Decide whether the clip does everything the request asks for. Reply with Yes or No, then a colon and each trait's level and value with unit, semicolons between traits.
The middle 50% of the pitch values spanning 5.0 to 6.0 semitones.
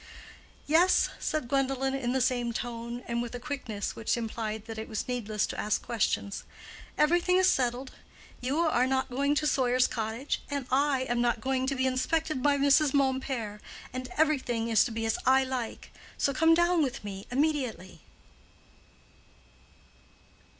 No: average, 3.3 semitones